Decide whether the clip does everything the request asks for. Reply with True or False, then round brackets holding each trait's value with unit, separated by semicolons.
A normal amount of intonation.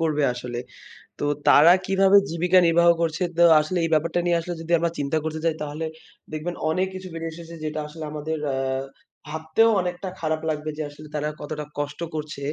False (2.1 semitones)